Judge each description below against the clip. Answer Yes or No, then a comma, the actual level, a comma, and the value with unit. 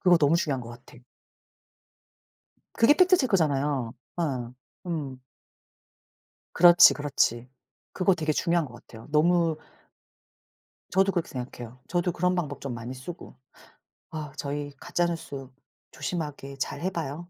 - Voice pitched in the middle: Yes, medium, 150 Hz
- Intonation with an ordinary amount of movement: Yes, average, 4.7 semitones